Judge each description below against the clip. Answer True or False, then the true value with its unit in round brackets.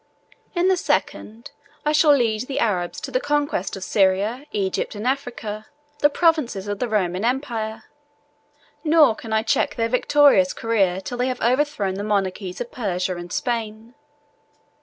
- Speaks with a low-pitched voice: False (225 Hz)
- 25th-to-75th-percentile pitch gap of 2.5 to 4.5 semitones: False (5.1 semitones)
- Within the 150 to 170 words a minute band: True (160 wpm)